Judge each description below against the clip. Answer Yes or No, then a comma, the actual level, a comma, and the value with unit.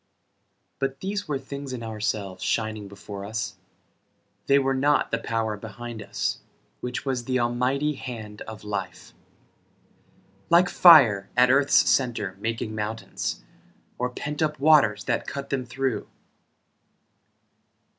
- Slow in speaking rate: Yes, slow, 125 wpm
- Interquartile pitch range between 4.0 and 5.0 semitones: Yes, average, 4.4 semitones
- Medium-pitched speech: No, low, 120 Hz